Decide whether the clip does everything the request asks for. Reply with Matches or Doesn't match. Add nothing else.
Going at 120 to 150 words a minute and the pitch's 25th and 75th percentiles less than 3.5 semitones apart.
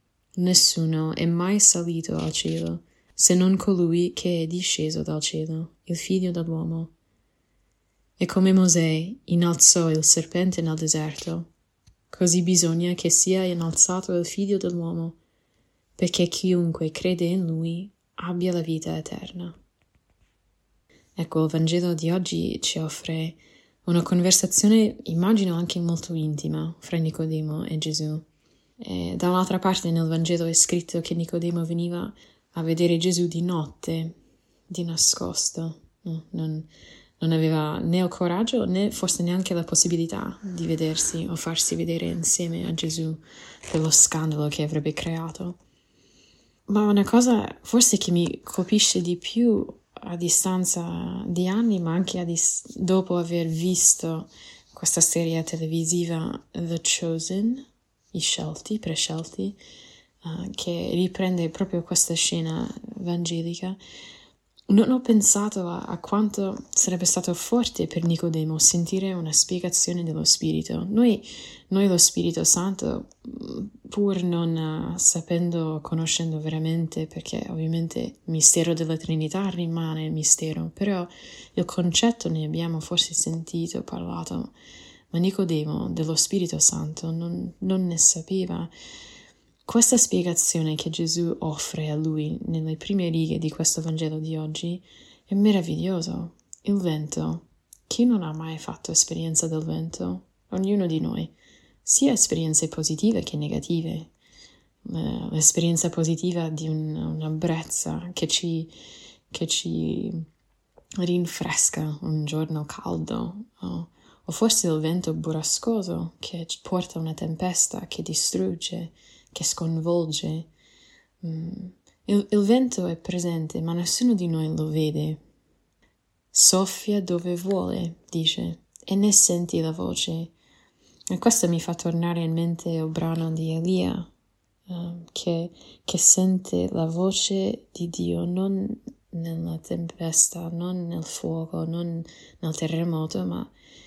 Matches